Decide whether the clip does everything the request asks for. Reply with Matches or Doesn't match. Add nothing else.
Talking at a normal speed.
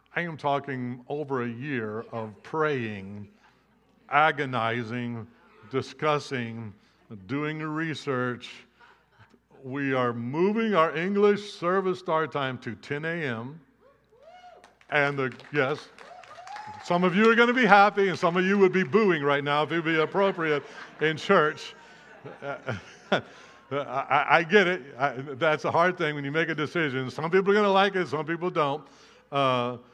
Matches